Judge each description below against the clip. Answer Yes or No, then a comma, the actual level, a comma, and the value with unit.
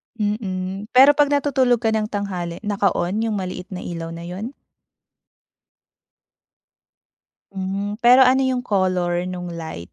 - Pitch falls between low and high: No, high, 200 Hz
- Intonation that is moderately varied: Yes, average, 4.4 semitones